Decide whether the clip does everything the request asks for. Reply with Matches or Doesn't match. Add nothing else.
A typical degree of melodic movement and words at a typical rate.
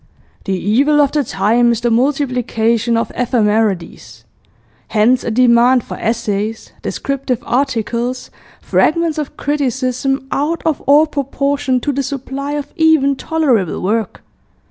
Doesn't match